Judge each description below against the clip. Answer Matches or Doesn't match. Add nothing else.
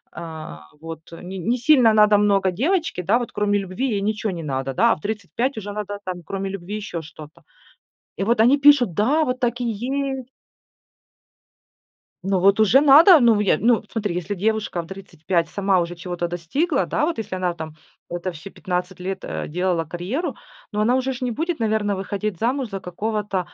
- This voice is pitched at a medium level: Doesn't match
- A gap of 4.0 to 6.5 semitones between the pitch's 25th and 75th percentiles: Matches